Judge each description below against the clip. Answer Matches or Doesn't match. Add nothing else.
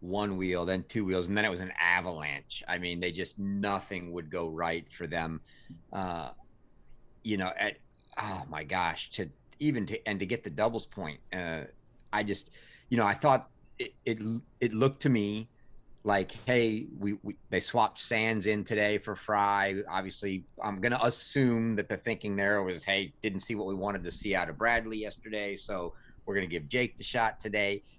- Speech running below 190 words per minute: Doesn't match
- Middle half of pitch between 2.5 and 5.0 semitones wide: Matches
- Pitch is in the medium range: Doesn't match